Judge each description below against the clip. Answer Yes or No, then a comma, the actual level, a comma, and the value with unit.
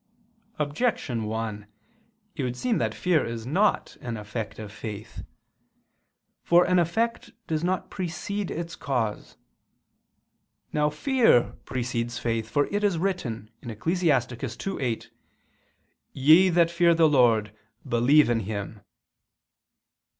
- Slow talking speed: Yes, slow, 115 wpm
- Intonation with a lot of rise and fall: Yes, wide, 7.2 semitones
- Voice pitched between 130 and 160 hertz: Yes, medium, 140 Hz